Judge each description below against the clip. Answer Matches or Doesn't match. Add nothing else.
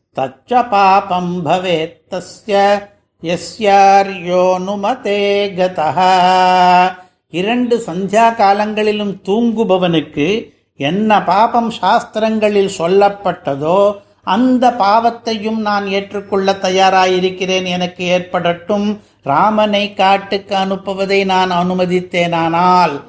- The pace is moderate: Doesn't match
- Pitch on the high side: Matches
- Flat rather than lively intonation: Matches